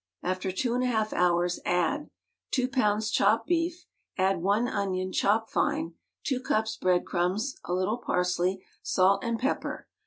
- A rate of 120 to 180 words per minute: Yes, average, 155 wpm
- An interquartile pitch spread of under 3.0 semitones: No, average, 4.8 semitones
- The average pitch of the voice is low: No, high, 200 Hz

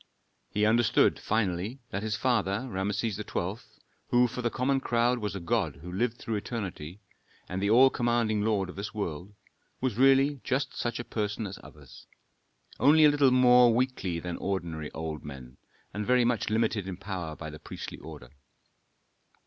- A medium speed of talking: Yes, average, 170 wpm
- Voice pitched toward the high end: No, low, 105 Hz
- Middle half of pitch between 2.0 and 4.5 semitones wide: No, average, 5.0 semitones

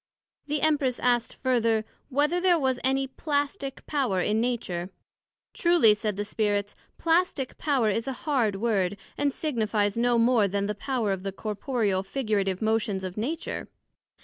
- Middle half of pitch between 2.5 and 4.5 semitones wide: No, average, 4.9 semitones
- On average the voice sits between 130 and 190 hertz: No, high, 230 Hz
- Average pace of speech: Yes, average, 150 wpm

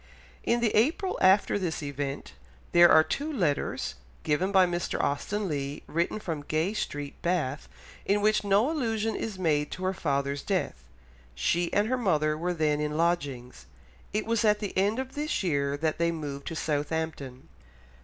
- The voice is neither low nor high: Yes, medium, 170 Hz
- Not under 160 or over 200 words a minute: Yes, average, 170 wpm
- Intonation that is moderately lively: No, wide, 5.9 semitones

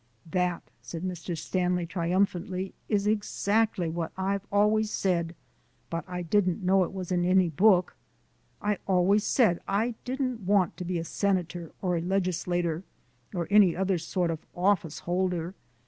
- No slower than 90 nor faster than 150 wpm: Yes, average, 145 wpm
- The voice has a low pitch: No, medium, 185 Hz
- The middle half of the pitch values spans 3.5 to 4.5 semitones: No, narrow, 2.4 semitones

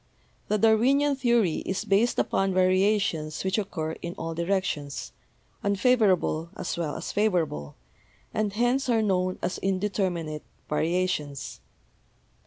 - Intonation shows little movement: No, average, 4.3 semitones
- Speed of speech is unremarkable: No, slow, 115 wpm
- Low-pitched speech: No, high, 190 Hz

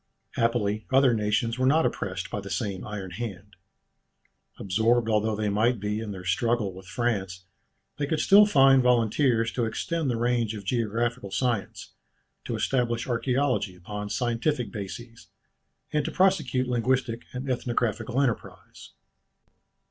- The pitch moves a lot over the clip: No, average, 3.4 semitones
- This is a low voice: Yes, low, 115 Hz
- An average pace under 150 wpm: Yes, average, 140 wpm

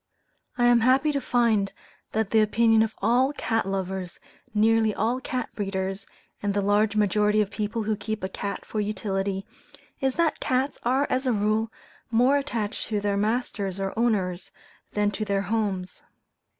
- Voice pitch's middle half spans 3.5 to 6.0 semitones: No, average, 2.9 semitones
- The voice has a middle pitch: No, high, 215 Hz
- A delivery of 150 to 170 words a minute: Yes, average, 165 wpm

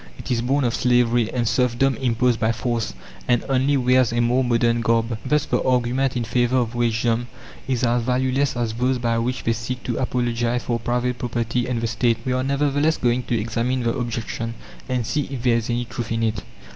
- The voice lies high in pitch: No, low, 120 Hz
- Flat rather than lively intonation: Yes, narrow, 1.7 semitones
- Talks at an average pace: No, fast, 210 wpm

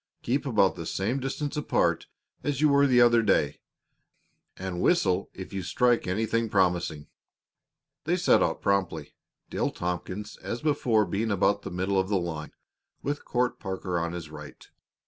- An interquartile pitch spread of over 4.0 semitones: Yes, average, 5.2 semitones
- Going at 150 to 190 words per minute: Yes, average, 160 wpm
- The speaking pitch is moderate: No, low, 100 Hz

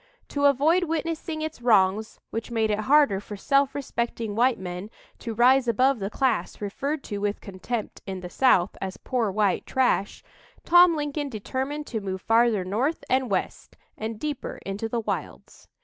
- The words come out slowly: No, average, 165 wpm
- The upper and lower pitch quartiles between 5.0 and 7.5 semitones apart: Yes, average, 5.3 semitones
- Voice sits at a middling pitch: No, high, 235 Hz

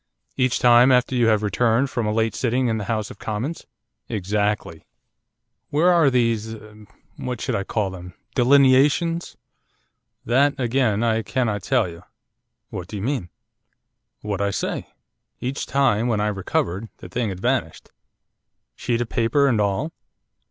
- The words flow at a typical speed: Yes, average, 150 wpm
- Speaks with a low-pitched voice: Yes, low, 115 Hz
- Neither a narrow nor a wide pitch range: Yes, average, 3.8 semitones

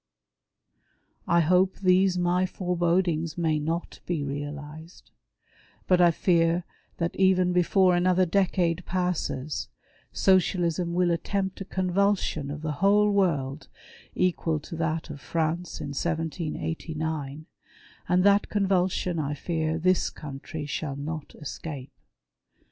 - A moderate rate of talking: No, slow, 115 wpm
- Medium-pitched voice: Yes, medium, 170 Hz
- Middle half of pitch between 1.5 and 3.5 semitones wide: Yes, average, 2.8 semitones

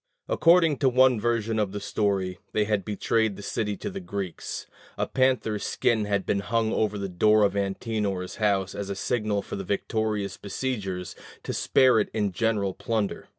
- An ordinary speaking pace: Yes, average, 180 wpm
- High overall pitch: No, low, 105 Hz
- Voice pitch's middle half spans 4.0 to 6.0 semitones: No, narrow, 2.4 semitones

